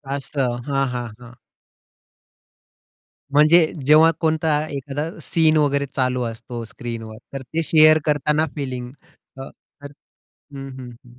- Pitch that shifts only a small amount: No, average, 3.8 semitones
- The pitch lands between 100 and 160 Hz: Yes, medium, 140 Hz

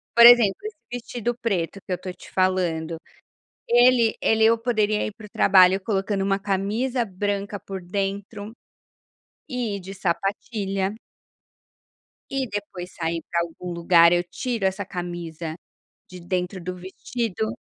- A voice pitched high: Yes, high, 195 Hz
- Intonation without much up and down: No, average, 3.5 semitones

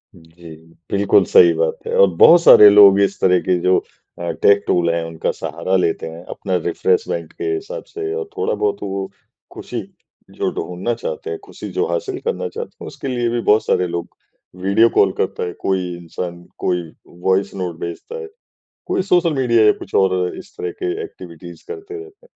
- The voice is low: Yes, low, 110 Hz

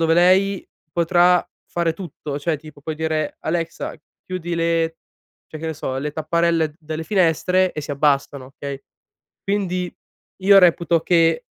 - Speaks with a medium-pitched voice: Yes, medium, 165 Hz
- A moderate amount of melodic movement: No, narrow, 2.3 semitones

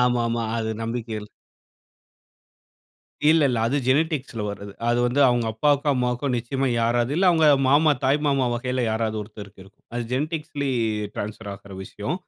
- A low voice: Yes, low, 120 Hz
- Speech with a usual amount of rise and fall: Yes, average, 4.1 semitones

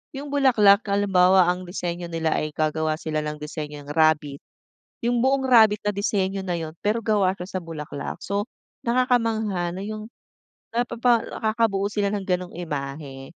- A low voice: No, high, 190 Hz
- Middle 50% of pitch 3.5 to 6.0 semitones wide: Yes, wide, 5.5 semitones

